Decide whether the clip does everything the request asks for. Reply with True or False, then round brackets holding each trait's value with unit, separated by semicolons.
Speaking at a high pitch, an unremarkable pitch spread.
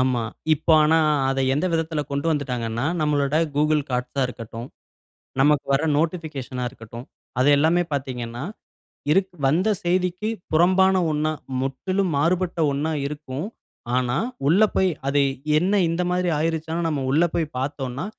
False (150 Hz; 4.1 semitones)